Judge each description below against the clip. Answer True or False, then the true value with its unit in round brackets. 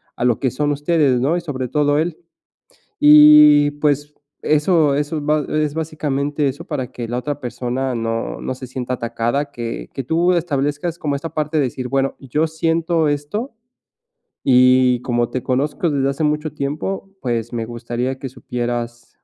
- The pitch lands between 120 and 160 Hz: True (140 Hz)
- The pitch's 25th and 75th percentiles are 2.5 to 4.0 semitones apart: True (3.2 semitones)